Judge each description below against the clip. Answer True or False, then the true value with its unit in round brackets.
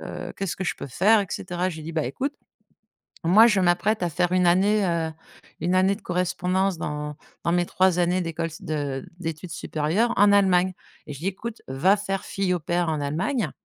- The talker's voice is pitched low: False (180 Hz)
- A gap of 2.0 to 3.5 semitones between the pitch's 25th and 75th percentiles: True (2.9 semitones)